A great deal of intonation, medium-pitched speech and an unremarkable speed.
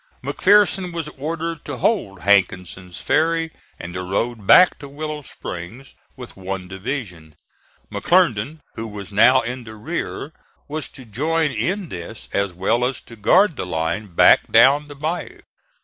No: wide, 8.1 semitones; low, 125 Hz; average, 150 wpm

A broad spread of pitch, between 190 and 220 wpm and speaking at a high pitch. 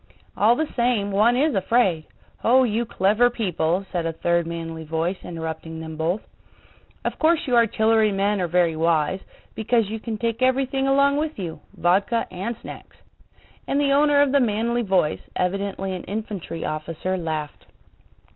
No: wide, 5.9 semitones; average, 155 wpm; high, 200 Hz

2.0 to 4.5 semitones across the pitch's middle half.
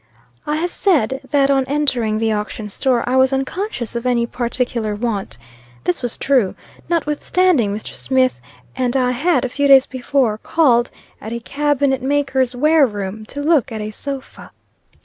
Yes: average, 3.5 semitones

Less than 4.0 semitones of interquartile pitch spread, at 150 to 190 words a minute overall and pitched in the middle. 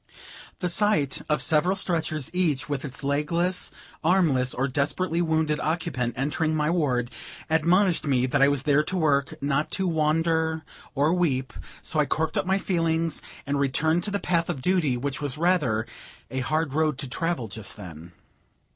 Yes: average, 3.5 semitones; average, 170 wpm; medium, 155 Hz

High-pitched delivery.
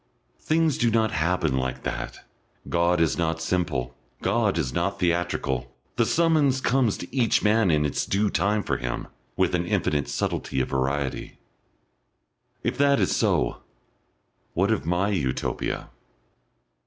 No: very low, 90 Hz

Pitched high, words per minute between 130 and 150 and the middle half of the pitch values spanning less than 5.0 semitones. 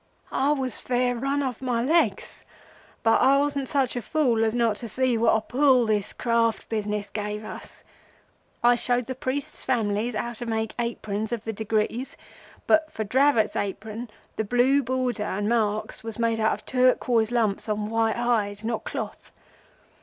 No: high, 235 Hz; average, 170 wpm; average, 2.8 semitones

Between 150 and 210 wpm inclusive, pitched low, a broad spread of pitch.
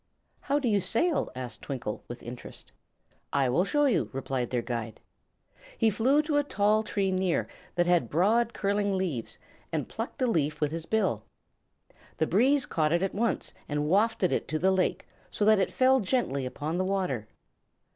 No: average, 180 wpm; medium, 185 Hz; wide, 7.2 semitones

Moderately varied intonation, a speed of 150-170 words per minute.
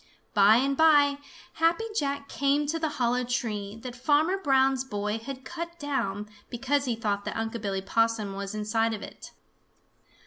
Yes: average, 4.9 semitones; average, 165 wpm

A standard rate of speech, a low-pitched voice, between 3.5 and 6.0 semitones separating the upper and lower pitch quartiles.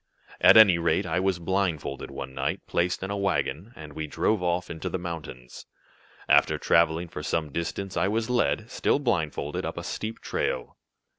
Yes: average, 175 wpm; very low, 85 Hz; average, 3.8 semitones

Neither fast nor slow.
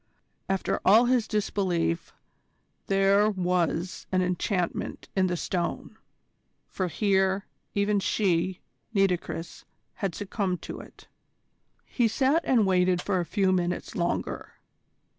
No: slow, 115 wpm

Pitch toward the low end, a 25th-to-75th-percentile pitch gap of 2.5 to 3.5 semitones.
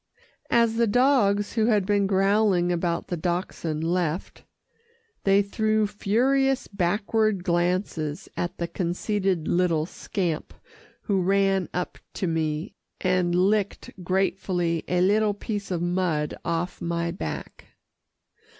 No: medium, 185 Hz; average, 3.0 semitones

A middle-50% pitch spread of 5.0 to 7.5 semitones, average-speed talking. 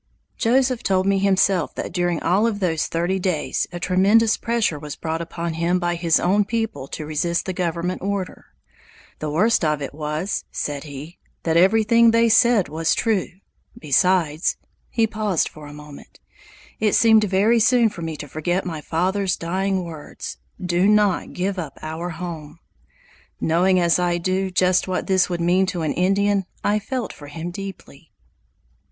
No: average, 3.5 semitones; average, 170 wpm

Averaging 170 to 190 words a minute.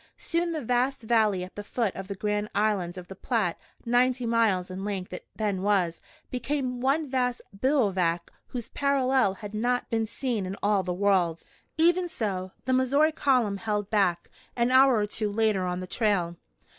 Yes: average, 180 wpm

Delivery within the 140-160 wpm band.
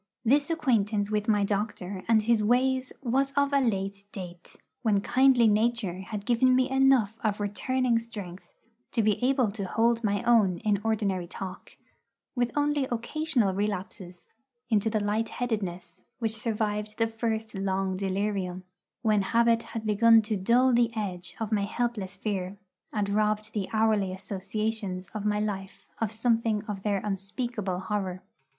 Yes: average, 155 wpm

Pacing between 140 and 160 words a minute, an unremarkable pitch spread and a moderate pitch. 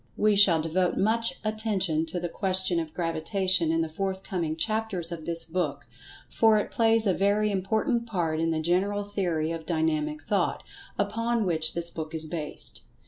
No: average, 170 wpm; average, 4.0 semitones; medium, 180 Hz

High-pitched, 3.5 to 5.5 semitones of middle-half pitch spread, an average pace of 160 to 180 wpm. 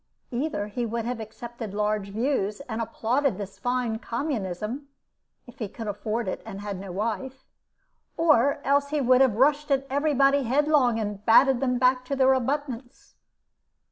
Yes: high, 245 Hz; average, 4.0 semitones; average, 165 wpm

